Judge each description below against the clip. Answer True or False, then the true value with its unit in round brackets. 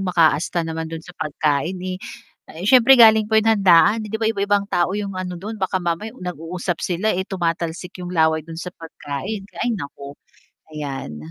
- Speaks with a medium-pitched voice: True (180 Hz)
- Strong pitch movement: False (3.8 semitones)